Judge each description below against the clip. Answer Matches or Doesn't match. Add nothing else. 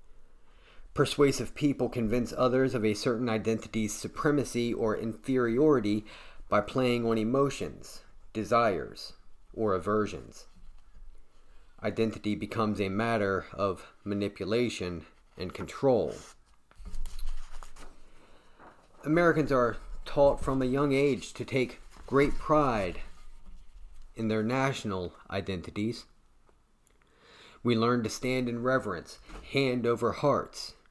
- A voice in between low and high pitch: Doesn't match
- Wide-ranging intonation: Doesn't match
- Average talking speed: Doesn't match